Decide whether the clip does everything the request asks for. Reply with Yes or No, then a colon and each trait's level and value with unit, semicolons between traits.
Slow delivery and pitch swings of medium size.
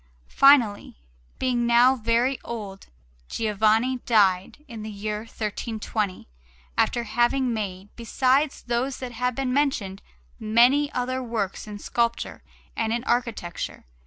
Yes: slow, 120 wpm; average, 3.0 semitones